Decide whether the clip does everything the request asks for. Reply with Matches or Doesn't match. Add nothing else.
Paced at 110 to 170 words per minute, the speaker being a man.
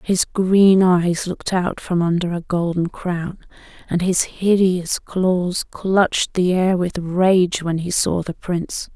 Doesn't match